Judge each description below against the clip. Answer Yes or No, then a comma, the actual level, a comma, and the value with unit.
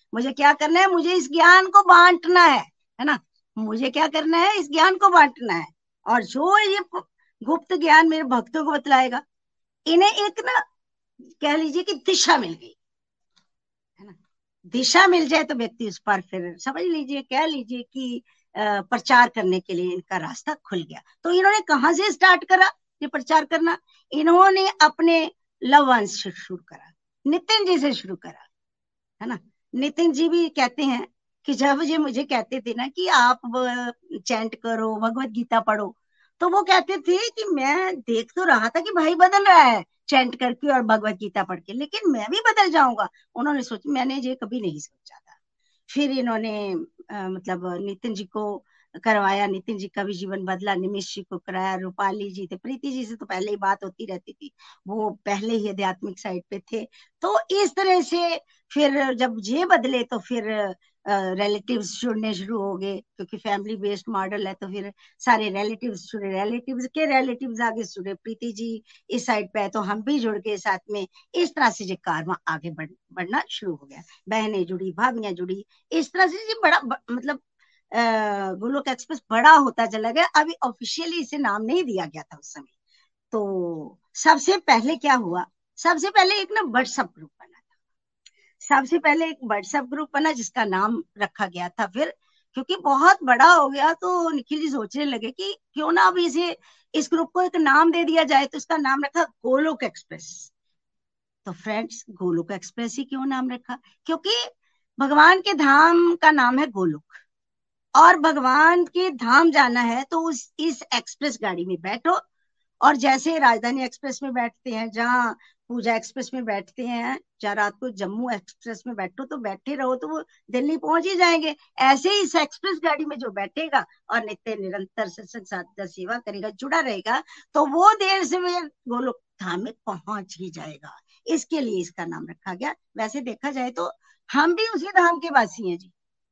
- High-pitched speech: Yes, very high, 255 Hz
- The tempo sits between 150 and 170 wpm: No, average, 180 wpm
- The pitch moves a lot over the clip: Yes, wide, 7.6 semitones